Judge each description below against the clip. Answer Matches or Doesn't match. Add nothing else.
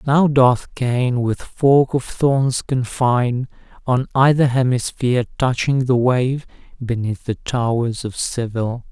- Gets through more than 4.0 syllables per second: Doesn't match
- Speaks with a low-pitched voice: Matches